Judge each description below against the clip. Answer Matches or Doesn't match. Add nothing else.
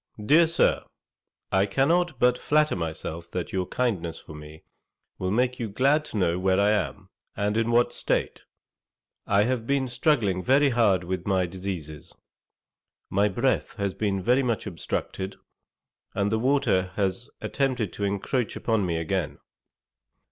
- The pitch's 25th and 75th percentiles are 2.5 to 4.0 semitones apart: Doesn't match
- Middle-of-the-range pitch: Doesn't match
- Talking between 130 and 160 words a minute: Matches